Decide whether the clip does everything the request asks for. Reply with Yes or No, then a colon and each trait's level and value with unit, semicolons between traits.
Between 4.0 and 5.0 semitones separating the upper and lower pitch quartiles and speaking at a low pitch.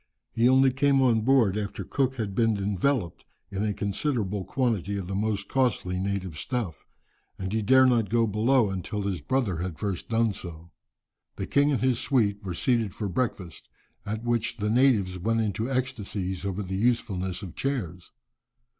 Yes: average, 4.4 semitones; low, 105 Hz